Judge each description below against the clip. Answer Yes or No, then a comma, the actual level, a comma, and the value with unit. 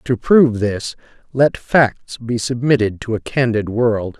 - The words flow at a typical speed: Yes, average, 155 wpm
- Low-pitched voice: Yes, low, 120 Hz